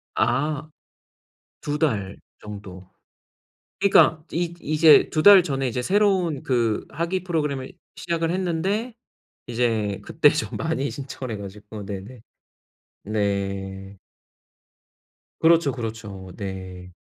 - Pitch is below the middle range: Yes, low, 130 Hz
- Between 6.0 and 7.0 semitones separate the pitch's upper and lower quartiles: No, wide, 8.2 semitones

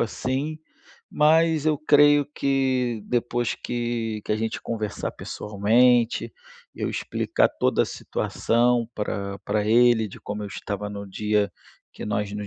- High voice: No, low, 115 Hz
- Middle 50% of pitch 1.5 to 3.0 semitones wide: No, average, 3.6 semitones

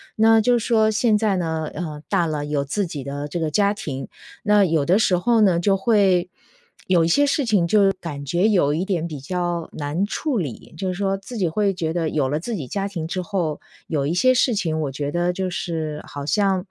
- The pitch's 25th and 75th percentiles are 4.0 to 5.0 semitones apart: Yes, average, 4.6 semitones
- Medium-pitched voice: Yes, medium, 175 Hz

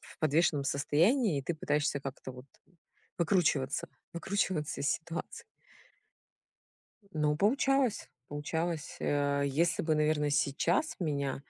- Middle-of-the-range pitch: Yes, medium, 155 Hz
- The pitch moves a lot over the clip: No, average, 3.3 semitones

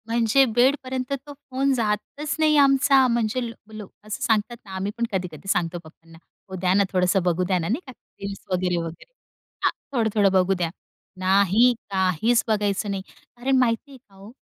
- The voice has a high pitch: Yes, high, 210 Hz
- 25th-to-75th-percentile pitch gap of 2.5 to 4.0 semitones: No, average, 5.2 semitones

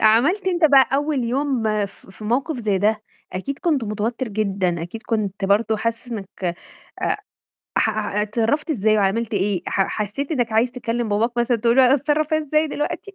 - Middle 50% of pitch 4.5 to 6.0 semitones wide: Yes, average, 4.9 semitones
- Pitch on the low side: No, high, 230 Hz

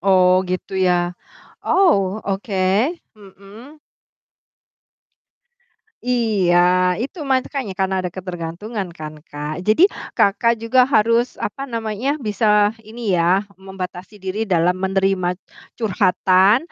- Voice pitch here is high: Yes, high, 195 Hz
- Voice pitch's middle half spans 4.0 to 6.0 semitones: No, average, 3.5 semitones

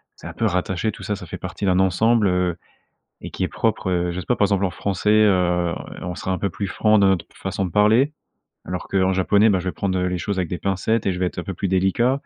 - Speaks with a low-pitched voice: Yes, very low, 95 Hz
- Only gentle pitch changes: Yes, narrow, 2.2 semitones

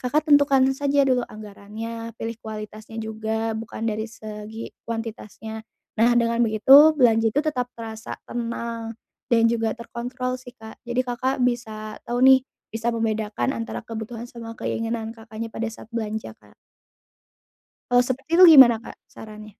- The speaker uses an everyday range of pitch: No, narrow, 1.9 semitones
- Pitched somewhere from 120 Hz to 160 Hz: No, high, 230 Hz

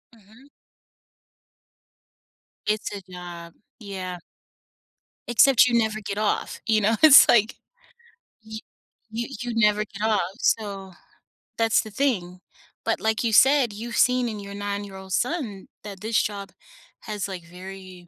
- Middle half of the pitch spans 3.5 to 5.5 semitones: No, average, 2.8 semitones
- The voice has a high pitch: Yes, high, 210 Hz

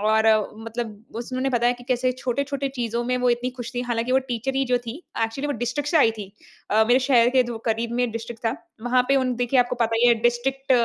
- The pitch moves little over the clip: Yes, narrow, 1.9 semitones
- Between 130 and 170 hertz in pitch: No, high, 245 Hz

